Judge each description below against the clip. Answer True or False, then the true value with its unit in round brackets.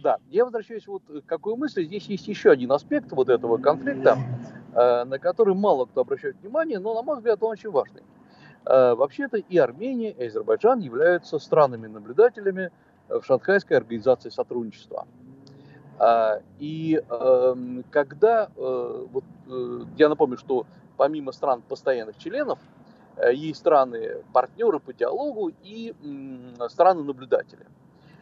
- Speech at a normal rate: True (120 wpm)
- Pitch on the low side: False (195 Hz)